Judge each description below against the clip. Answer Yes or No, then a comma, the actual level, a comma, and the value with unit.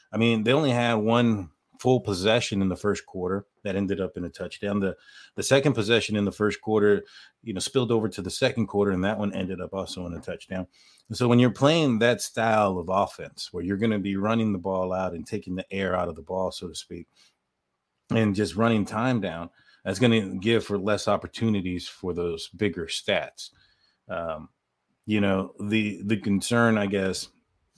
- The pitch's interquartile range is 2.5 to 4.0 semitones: Yes, average, 3.1 semitones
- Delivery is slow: No, fast, 205 wpm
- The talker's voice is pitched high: No, low, 100 Hz